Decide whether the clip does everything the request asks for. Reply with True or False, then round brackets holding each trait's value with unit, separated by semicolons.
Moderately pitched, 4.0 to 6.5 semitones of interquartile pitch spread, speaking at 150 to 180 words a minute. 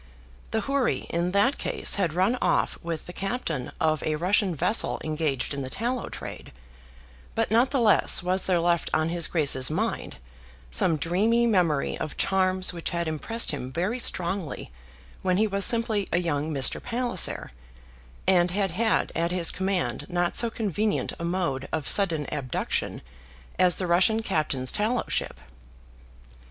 True (180 Hz; 4.6 semitones; 160 wpm)